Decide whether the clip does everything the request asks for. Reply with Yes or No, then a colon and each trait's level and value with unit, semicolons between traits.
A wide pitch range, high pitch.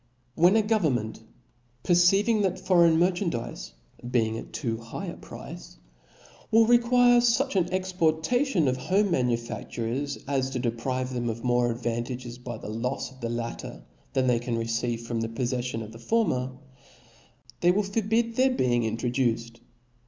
No: wide, 8.1 semitones; low, 130 Hz